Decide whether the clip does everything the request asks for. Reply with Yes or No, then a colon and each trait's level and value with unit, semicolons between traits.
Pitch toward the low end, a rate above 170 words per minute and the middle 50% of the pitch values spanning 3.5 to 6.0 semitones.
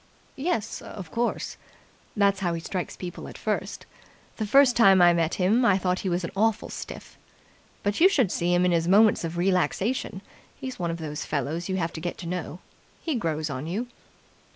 No: medium, 185 Hz; average, 200 wpm; average, 4.0 semitones